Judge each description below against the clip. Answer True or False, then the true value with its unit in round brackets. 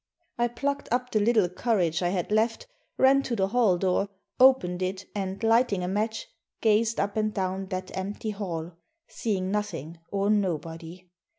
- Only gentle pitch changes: False (3.5 semitones)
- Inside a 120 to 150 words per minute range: False (165 wpm)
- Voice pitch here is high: True (200 Hz)